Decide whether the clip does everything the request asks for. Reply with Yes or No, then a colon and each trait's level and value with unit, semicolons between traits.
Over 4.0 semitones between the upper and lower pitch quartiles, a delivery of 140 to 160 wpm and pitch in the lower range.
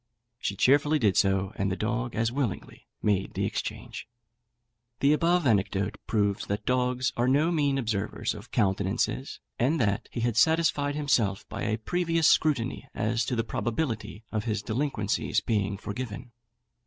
Yes: average, 5.1 semitones; average, 155 wpm; low, 115 Hz